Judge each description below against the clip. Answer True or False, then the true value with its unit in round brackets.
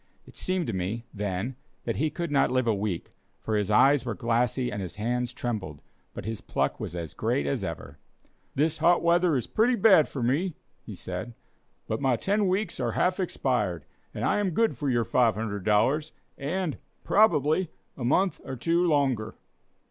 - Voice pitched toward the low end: True (130 Hz)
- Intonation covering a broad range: True (7.7 semitones)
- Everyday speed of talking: True (180 wpm)